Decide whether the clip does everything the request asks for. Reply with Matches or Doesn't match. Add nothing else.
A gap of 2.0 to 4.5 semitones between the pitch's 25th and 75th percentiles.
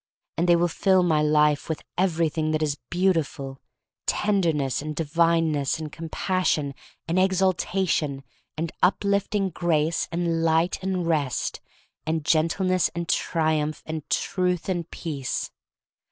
Matches